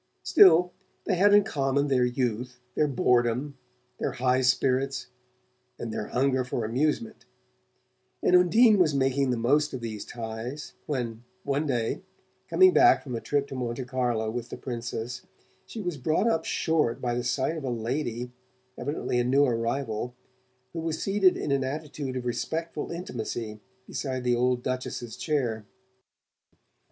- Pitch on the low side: Yes, low, 130 Hz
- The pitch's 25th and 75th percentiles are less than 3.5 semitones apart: No, average, 3.8 semitones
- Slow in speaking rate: No, average, 155 wpm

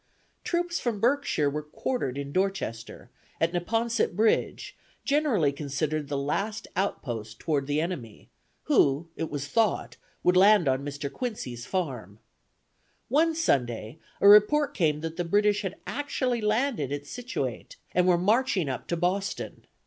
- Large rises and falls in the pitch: Yes, wide, 7.7 semitones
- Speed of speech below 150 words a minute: Yes, average, 140 wpm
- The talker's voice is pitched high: No, medium, 175 Hz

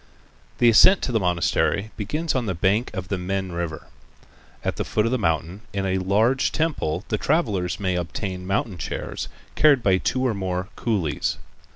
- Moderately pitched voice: No, low, 100 Hz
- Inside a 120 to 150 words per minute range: No, average, 180 wpm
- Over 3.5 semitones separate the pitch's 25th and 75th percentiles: Yes, average, 4.3 semitones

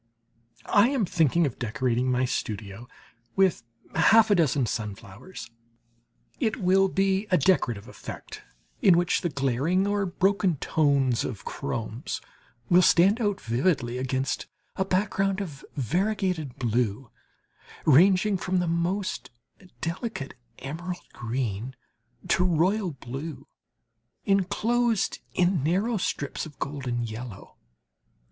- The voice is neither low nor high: Yes, medium, 165 Hz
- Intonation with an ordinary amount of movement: No, wide, 7.1 semitones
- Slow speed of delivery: Yes, slow, 115 wpm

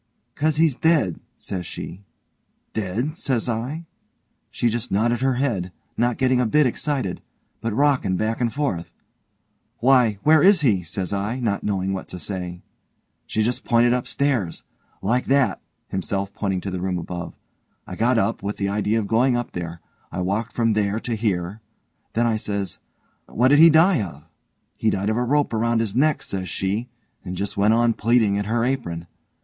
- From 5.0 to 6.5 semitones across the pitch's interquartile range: No, average, 4.4 semitones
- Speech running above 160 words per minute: Yes, average, 180 wpm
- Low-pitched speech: Yes, low, 110 Hz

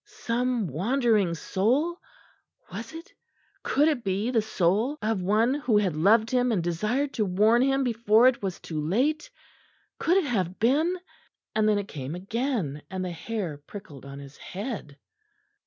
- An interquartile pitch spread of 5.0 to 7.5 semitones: Yes, wide, 5.5 semitones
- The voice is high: Yes, high, 215 Hz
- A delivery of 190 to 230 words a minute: No, average, 160 wpm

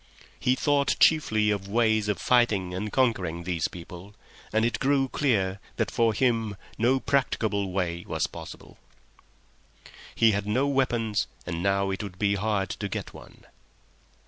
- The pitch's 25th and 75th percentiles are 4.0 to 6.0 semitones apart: No, average, 3.6 semitones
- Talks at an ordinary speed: Yes, average, 150 wpm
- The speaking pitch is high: No, low, 105 Hz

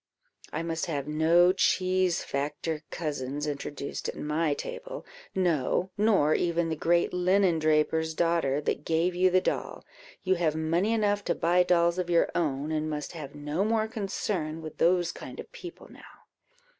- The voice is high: No, medium, 170 Hz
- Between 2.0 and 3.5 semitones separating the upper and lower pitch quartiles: Yes, average, 3.2 semitones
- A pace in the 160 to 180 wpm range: Yes, average, 165 wpm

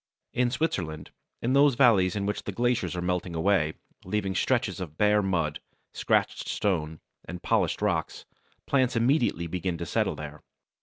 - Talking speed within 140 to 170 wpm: Yes, average, 160 wpm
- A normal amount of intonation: No, wide, 5.8 semitones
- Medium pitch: No, very low, 95 Hz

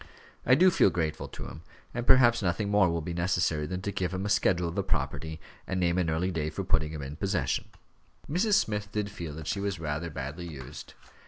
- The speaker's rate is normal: No, fast, 225 wpm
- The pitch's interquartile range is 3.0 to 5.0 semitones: Yes, average, 4.2 semitones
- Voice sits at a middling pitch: No, very low, 90 Hz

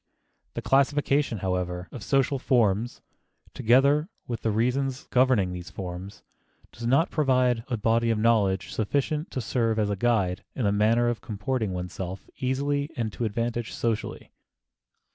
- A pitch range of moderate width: Yes, average, 4.3 semitones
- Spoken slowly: No, average, 145 wpm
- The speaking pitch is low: Yes, low, 115 Hz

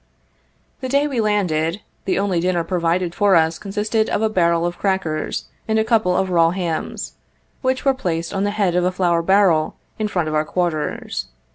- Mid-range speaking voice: Yes, medium, 180 Hz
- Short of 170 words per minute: No, average, 190 wpm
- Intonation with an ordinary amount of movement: Yes, average, 3.7 semitones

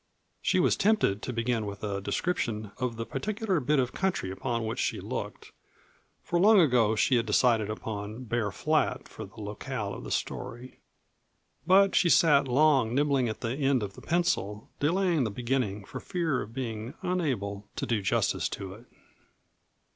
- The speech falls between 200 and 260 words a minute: No, average, 170 wpm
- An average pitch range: No, wide, 5.9 semitones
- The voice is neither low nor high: No, low, 120 Hz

